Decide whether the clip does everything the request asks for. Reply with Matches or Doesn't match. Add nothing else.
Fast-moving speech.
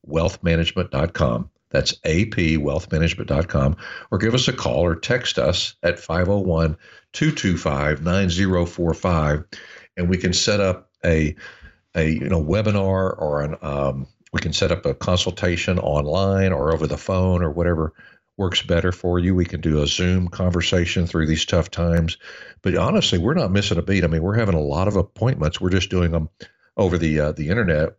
Doesn't match